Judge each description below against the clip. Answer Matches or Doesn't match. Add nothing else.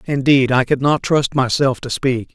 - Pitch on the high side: Doesn't match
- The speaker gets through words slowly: Doesn't match